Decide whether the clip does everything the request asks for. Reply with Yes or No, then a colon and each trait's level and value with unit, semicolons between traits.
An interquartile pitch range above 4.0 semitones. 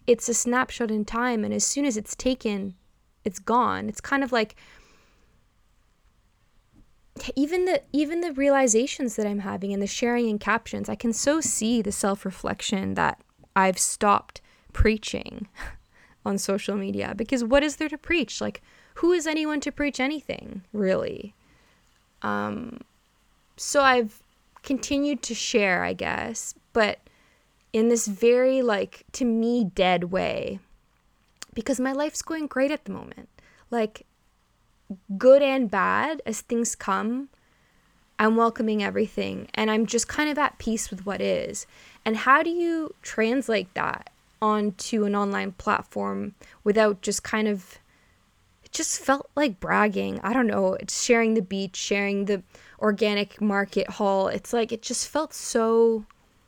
Yes: average, 4.5 semitones